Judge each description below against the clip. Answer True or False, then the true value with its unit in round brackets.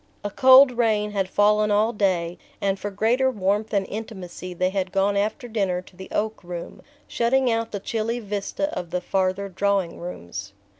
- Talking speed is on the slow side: False (180 wpm)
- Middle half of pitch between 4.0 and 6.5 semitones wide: False (2.9 semitones)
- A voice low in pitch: False (205 Hz)